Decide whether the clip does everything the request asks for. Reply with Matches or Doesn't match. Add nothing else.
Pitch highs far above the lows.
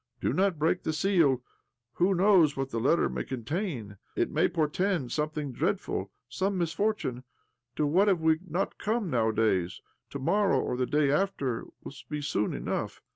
Matches